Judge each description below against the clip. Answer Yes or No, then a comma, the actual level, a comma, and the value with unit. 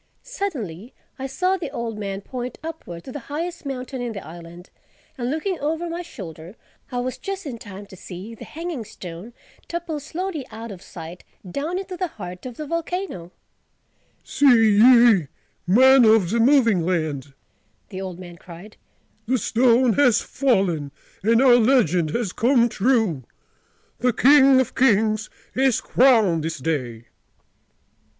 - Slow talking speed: No, average, 150 wpm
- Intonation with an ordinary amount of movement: No, wide, 6.8 semitones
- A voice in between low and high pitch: No, high, 235 Hz